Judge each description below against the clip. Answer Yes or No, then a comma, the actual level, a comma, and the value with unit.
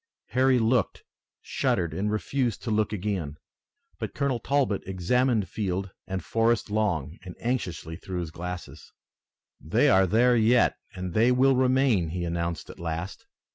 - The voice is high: No, low, 105 Hz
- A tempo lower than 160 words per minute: Yes, average, 145 wpm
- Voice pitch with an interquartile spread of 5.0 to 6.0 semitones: Yes, wide, 5.6 semitones